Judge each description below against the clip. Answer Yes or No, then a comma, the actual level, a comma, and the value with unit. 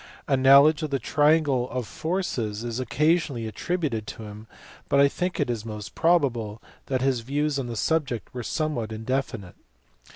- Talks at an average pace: Yes, average, 170 wpm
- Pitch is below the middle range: Yes, low, 130 Hz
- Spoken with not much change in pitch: No, average, 5.0 semitones